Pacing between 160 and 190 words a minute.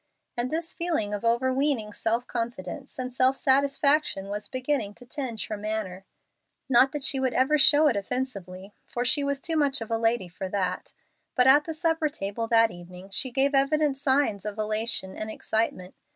Yes: average, 180 wpm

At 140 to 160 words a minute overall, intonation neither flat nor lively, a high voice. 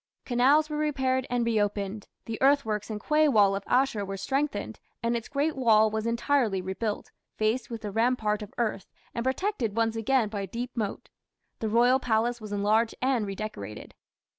No: average, 175 wpm; average, 3.6 semitones; high, 230 Hz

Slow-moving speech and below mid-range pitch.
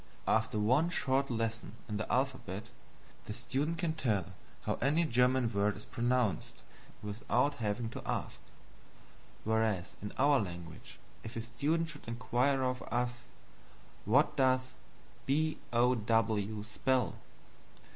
Yes: slow, 125 wpm; low, 120 Hz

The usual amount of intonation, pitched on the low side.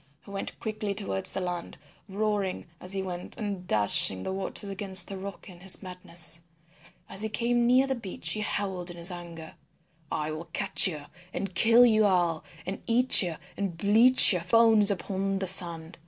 No: average, 3.2 semitones; high, 190 Hz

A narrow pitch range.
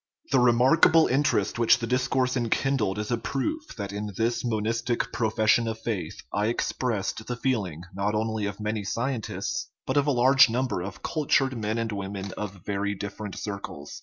No: average, 3.6 semitones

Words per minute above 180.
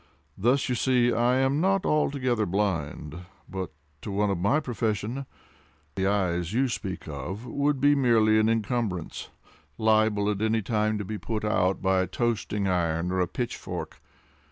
No: average, 160 wpm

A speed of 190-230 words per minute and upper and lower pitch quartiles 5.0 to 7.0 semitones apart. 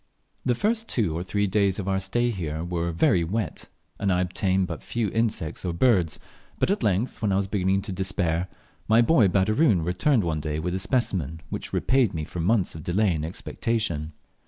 No: average, 200 wpm; average, 4.5 semitones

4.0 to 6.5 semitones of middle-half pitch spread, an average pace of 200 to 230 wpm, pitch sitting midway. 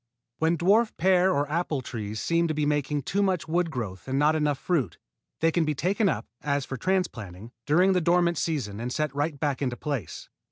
Yes: average, 4.4 semitones; fast, 205 wpm; medium, 150 Hz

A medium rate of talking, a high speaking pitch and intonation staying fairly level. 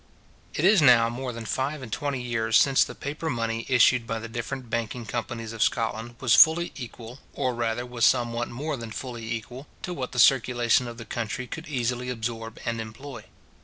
No: average, 195 wpm; low, 120 Hz; narrow, 2.3 semitones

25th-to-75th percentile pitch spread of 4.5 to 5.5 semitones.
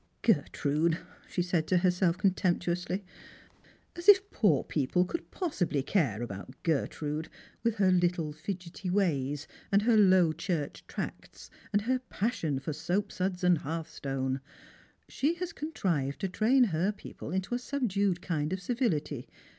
Yes: average, 4.8 semitones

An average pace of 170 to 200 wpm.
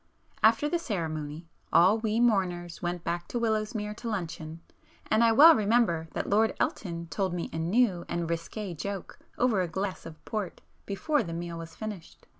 Yes: average, 175 wpm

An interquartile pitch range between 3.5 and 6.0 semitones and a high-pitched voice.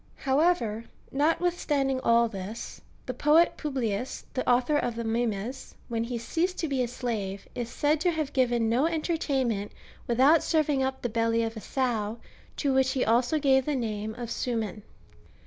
Yes: average, 4.1 semitones; very high, 250 Hz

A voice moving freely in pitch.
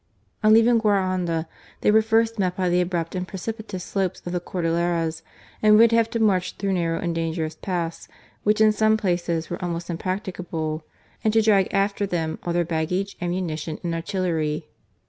No: average, 3.8 semitones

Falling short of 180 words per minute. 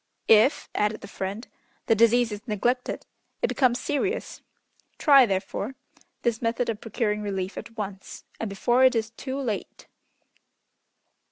Yes: average, 140 wpm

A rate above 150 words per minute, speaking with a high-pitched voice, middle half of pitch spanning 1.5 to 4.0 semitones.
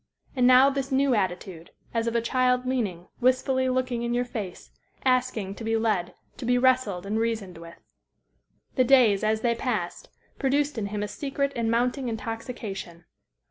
Yes: average, 170 wpm; high, 235 Hz; average, 3.7 semitones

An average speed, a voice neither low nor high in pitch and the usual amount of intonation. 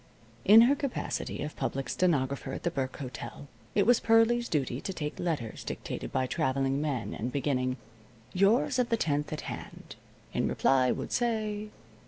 No: average, 165 wpm; medium, 150 Hz; wide, 8.3 semitones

